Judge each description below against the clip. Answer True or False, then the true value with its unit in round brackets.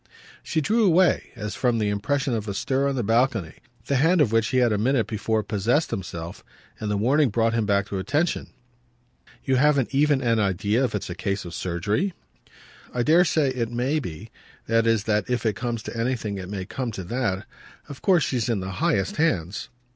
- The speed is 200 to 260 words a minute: True (205 wpm)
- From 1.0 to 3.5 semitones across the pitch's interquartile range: False (4.8 semitones)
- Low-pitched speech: True (115 Hz)